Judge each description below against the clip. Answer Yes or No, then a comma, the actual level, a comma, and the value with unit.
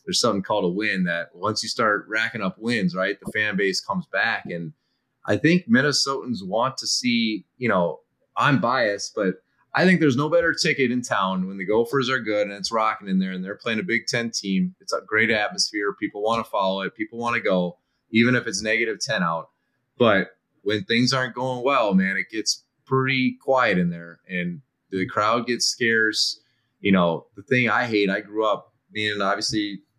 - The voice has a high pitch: No, low, 110 Hz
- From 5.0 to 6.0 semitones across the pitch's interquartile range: Yes, average, 5.3 semitones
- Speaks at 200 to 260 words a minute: Yes, fast, 205 wpm